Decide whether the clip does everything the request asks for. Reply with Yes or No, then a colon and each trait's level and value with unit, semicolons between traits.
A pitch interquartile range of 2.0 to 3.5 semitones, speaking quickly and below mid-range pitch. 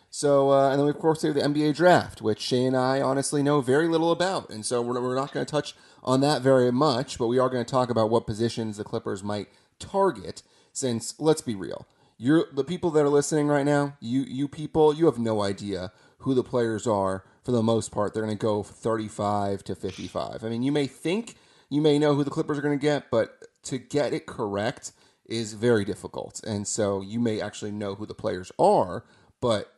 No: average, 5.0 semitones; fast, 230 wpm; low, 130 Hz